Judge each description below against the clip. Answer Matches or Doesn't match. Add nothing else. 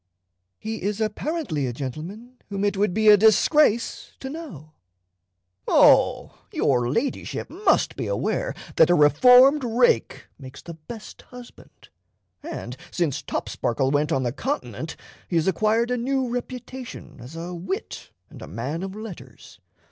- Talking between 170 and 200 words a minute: Doesn't match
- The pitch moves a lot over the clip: Matches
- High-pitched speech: Matches